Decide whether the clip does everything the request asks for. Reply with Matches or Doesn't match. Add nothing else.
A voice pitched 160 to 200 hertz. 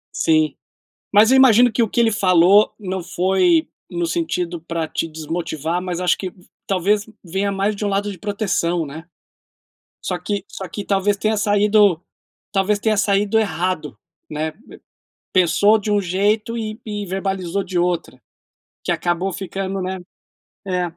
Matches